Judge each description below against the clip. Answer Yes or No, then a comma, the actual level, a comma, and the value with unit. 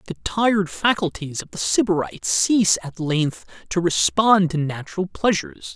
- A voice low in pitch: No, medium, 165 Hz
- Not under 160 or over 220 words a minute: No, average, 145 wpm